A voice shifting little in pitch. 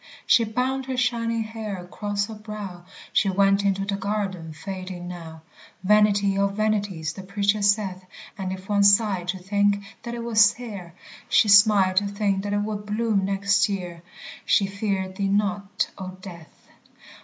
Yes: narrow, 1.9 semitones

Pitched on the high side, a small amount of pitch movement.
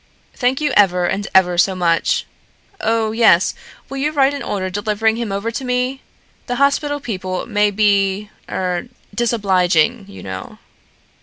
No: high, 210 Hz; average, 4.8 semitones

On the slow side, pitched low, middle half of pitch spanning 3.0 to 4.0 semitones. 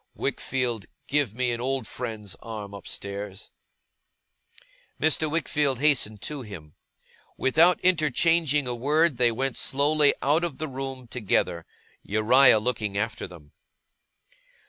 No: slow, 120 wpm; low, 125 Hz; wide, 5.5 semitones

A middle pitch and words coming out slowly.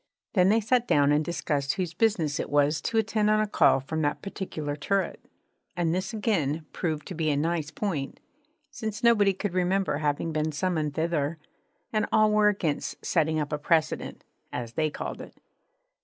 No: medium, 165 Hz; average, 180 wpm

